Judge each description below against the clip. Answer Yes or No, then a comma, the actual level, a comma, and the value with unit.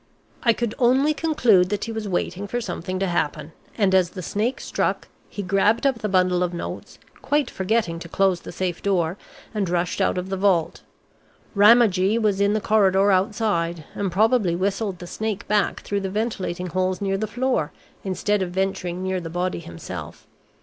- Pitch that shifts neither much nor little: Yes, average, 3.0 semitones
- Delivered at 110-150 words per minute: No, average, 185 wpm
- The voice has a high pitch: Yes, high, 195 Hz